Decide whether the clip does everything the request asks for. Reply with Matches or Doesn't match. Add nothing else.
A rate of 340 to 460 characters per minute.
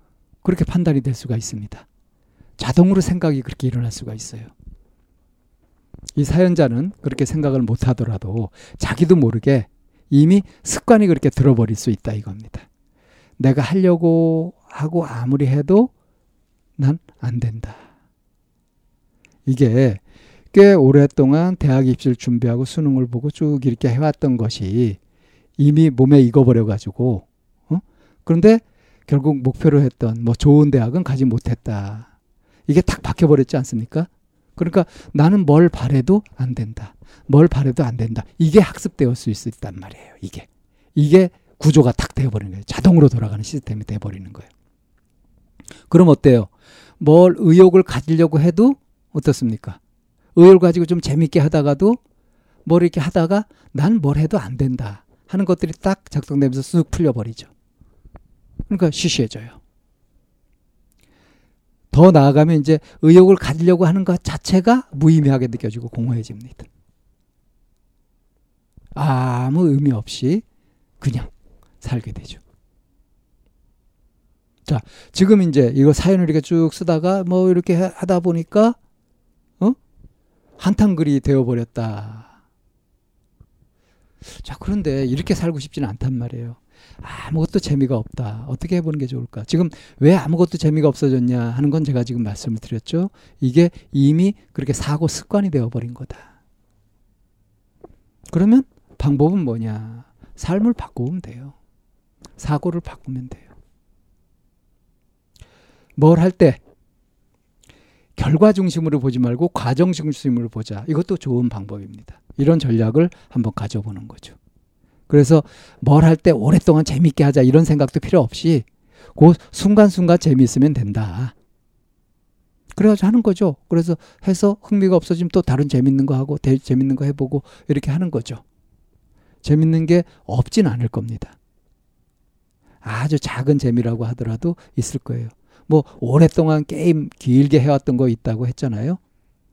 Doesn't match